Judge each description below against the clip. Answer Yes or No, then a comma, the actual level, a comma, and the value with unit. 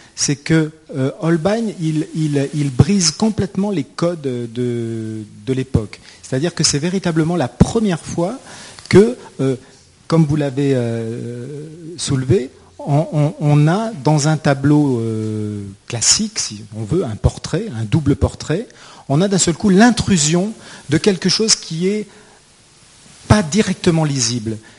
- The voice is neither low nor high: Yes, medium, 150 Hz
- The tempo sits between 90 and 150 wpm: Yes, slow, 145 wpm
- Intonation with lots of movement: Yes, wide, 6.2 semitones